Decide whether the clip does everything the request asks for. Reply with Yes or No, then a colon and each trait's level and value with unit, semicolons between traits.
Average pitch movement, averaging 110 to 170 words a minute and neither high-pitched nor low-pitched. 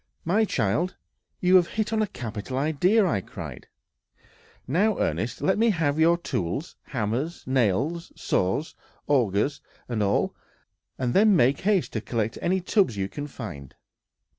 No: wide, 8.4 semitones; average, 145 wpm; medium, 145 Hz